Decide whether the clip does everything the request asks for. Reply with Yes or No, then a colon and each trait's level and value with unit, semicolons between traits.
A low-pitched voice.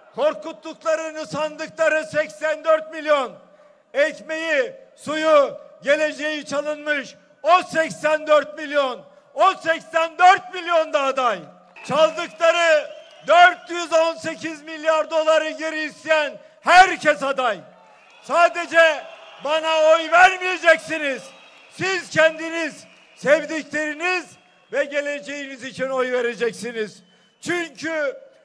No: very high, 310 Hz